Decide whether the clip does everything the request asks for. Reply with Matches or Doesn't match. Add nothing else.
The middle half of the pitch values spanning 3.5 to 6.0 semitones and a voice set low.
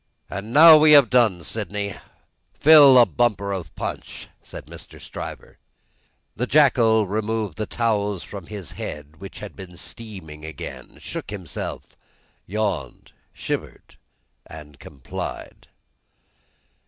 Matches